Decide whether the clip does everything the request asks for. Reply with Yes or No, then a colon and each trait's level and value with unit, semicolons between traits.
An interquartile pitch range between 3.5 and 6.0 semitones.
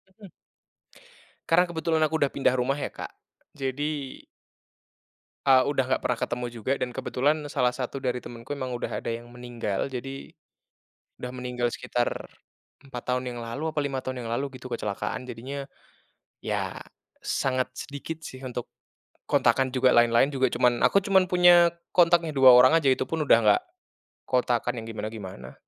No: average, 2.7 semitones